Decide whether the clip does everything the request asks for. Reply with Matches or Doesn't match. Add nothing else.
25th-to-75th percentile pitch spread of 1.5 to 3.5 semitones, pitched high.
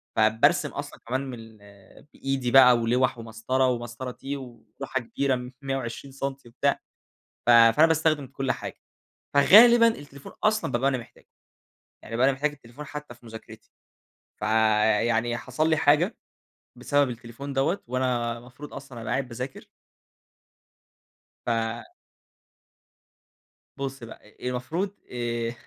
Doesn't match